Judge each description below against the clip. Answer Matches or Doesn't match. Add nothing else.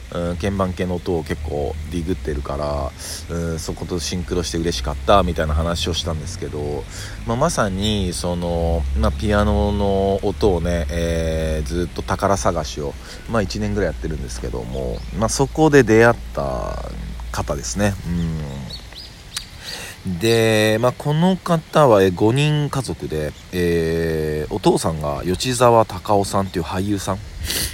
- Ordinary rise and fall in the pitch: Matches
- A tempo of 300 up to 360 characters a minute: Doesn't match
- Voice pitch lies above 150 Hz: Doesn't match